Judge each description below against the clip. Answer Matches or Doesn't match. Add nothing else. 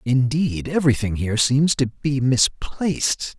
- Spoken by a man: Matches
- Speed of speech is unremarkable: Doesn't match